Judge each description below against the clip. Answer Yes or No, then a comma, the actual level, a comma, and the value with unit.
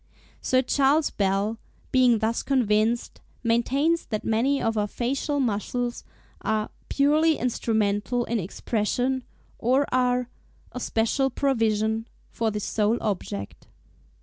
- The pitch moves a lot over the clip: No, average, 3.1 semitones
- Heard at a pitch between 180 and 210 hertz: No, high, 235 Hz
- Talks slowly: Yes, slow, 115 wpm